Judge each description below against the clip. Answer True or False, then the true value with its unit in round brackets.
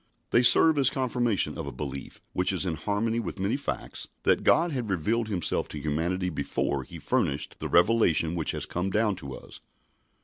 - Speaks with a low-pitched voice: True (95 Hz)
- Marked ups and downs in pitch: True (6.0 semitones)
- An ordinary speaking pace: True (190 wpm)